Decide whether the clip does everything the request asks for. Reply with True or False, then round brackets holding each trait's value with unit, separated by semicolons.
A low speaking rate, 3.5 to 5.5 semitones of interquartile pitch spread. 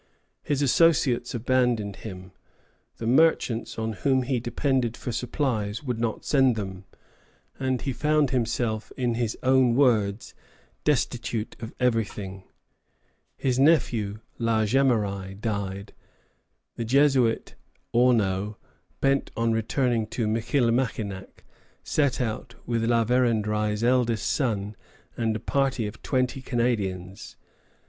False (115 wpm; 3.1 semitones)